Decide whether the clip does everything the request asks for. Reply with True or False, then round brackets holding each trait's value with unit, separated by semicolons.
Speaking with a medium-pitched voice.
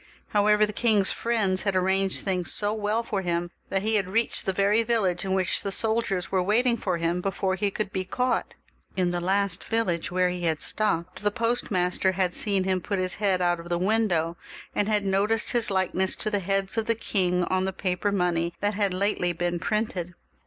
False (195 Hz)